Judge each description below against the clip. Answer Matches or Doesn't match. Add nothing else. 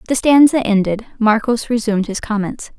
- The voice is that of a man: Doesn't match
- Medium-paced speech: Matches